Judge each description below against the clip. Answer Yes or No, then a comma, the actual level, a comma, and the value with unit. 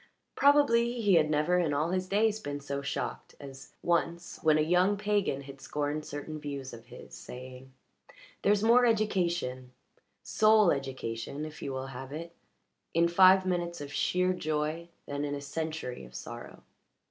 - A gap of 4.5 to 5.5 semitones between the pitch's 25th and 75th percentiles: Yes, average, 4.9 semitones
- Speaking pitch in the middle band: Yes, medium, 155 Hz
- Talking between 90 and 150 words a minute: No, average, 160 wpm